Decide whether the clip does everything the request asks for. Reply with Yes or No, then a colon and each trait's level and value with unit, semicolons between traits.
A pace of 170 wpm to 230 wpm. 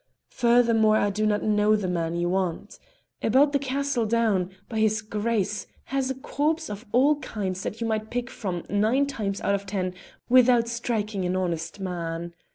Yes: average, 175 wpm